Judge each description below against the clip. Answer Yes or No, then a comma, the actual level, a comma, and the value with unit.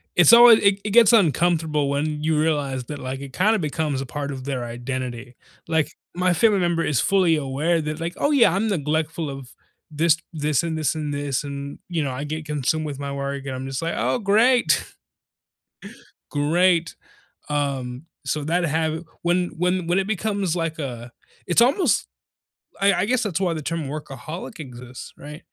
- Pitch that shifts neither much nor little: Yes, average, 4.0 semitones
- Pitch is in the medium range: Yes, medium, 155 Hz